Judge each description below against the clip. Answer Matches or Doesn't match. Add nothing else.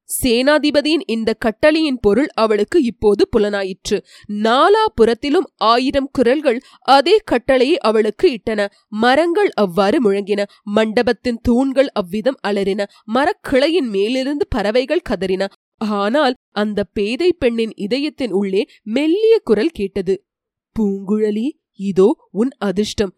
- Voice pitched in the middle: Doesn't match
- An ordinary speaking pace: Matches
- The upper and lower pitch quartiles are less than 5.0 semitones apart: Doesn't match